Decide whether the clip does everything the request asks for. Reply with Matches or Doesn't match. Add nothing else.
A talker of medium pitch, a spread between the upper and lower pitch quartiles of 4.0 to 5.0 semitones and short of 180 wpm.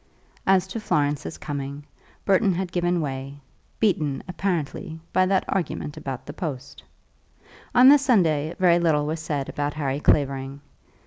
Matches